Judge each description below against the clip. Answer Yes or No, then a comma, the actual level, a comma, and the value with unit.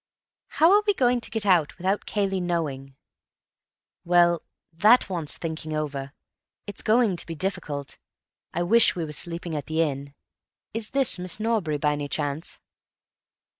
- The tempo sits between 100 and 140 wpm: No, average, 155 wpm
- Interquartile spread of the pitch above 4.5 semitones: Yes, wide, 5.5 semitones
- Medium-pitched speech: Yes, medium, 170 Hz